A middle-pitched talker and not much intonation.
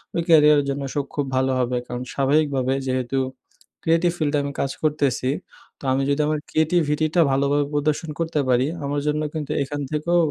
Yes: medium, 145 Hz; narrow, 2.3 semitones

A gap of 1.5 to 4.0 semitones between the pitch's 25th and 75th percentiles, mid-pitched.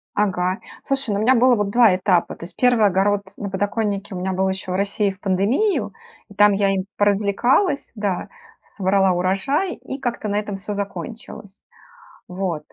No: average, 2.7 semitones; high, 200 Hz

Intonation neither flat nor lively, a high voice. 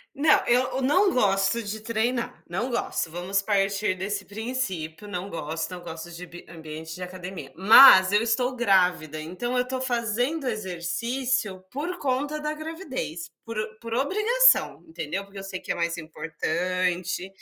No: wide, 6.0 semitones; high, 200 Hz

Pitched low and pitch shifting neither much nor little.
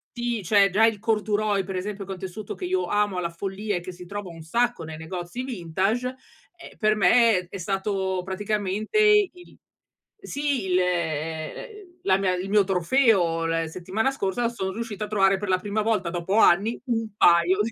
No: high, 200 Hz; average, 3.7 semitones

